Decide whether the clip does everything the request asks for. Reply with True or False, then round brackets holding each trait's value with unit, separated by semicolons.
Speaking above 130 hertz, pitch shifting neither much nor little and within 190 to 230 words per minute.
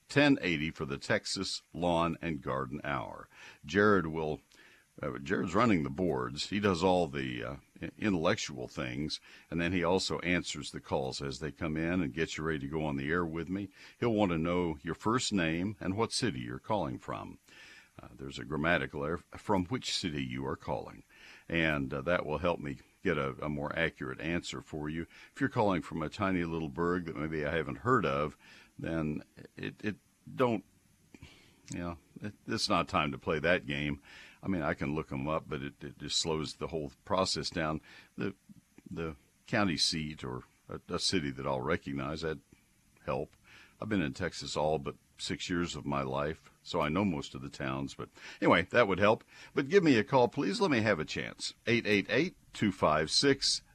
False (80 Hz; 3.6 semitones; 195 wpm)